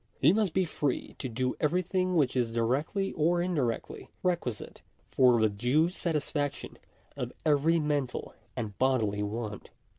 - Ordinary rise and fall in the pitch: No, wide, 5.9 semitones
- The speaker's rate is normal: Yes, average, 145 wpm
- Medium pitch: Yes, medium, 145 Hz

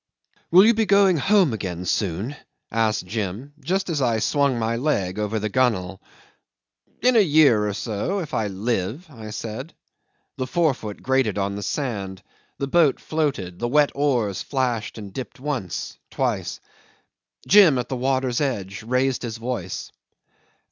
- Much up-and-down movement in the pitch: Yes, wide, 5.7 semitones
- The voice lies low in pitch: Yes, low, 120 Hz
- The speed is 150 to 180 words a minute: Yes, average, 155 wpm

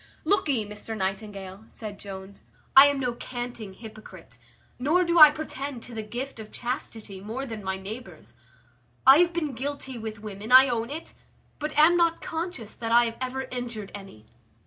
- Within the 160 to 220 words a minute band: Yes, average, 170 wpm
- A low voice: No, high, 235 Hz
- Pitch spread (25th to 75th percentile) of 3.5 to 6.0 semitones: Yes, average, 4.7 semitones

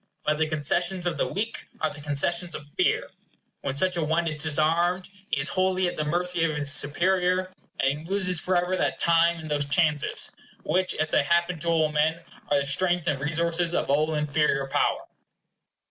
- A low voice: No, medium, 165 Hz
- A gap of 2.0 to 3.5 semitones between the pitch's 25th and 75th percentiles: Yes, average, 2.9 semitones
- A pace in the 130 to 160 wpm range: No, average, 190 wpm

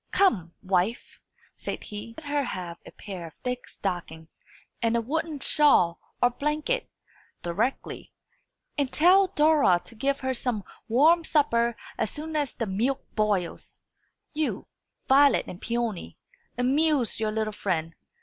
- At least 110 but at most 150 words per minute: Yes, average, 140 wpm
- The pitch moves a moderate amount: No, wide, 6.5 semitones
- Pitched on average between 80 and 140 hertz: No, high, 240 Hz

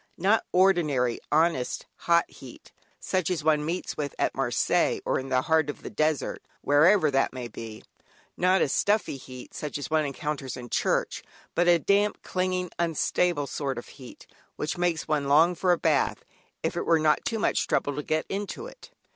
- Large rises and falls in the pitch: No, average, 4.1 semitones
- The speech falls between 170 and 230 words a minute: Yes, average, 190 wpm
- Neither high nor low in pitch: Yes, medium, 155 Hz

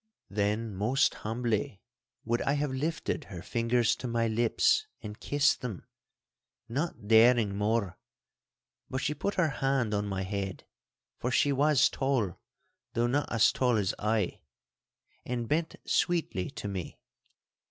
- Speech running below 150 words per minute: Yes, average, 140 wpm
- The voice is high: No, low, 115 Hz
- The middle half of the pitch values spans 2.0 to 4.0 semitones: No, average, 4.6 semitones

